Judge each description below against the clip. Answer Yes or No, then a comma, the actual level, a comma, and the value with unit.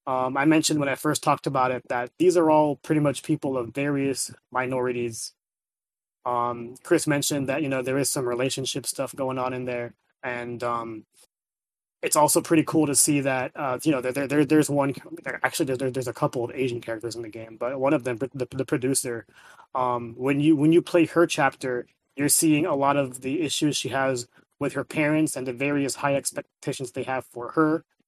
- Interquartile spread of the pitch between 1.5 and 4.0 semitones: Yes, average, 3.0 semitones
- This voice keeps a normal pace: No, fast, 215 wpm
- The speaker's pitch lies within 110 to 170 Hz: Yes, low, 135 Hz